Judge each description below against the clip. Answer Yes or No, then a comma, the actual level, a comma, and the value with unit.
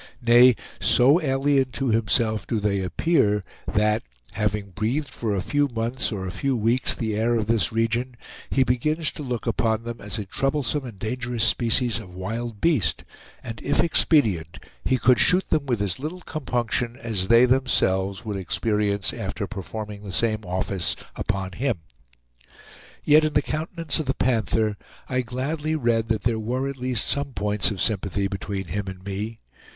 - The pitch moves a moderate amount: Yes, average, 4.1 semitones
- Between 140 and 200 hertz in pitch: No, low, 115 Hz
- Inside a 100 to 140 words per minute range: No, average, 170 wpm